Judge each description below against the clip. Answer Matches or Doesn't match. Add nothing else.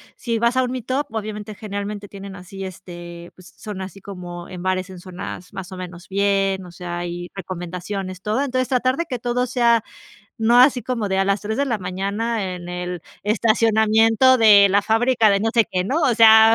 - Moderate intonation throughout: Matches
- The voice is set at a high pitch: Matches